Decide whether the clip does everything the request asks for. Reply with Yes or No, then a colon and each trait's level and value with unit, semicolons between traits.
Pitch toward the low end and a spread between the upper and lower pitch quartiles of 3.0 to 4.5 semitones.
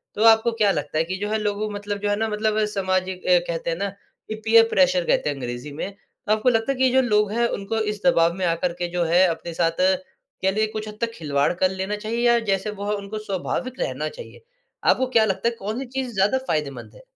No: high, 205 Hz; average, 3.5 semitones